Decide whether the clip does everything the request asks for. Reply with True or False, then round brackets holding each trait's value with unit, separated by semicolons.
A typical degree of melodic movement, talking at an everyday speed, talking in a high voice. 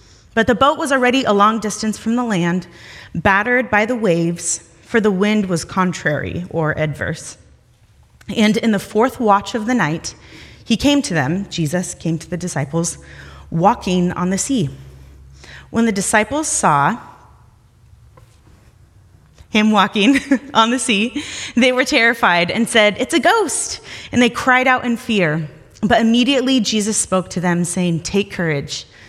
False (6.6 semitones; 155 wpm; 200 Hz)